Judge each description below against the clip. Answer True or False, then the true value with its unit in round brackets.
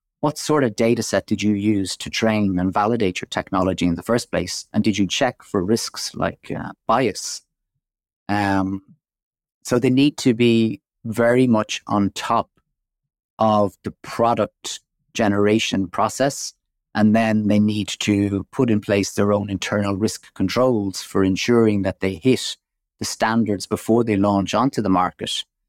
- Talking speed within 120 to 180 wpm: True (160 wpm)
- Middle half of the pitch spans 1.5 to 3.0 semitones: True (2.6 semitones)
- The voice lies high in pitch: False (105 Hz)